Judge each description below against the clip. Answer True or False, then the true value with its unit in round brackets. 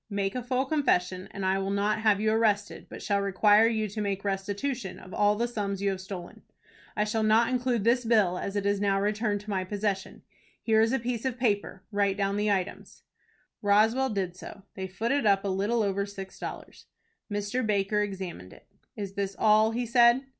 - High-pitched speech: True (205 Hz)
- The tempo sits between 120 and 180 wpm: False (205 wpm)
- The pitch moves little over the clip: True (2.3 semitones)